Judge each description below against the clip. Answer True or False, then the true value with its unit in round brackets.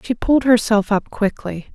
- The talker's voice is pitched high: True (225 Hz)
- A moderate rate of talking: True (170 wpm)